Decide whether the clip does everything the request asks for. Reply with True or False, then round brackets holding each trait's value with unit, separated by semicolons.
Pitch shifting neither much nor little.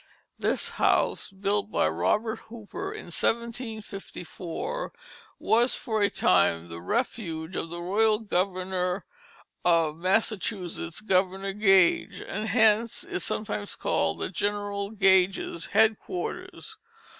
True (3.8 semitones)